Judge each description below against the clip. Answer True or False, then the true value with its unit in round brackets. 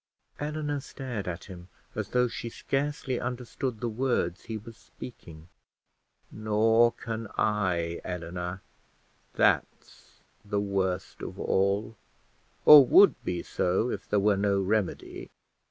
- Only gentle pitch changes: False (4.6 semitones)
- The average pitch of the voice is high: False (105 Hz)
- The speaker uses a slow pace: True (120 wpm)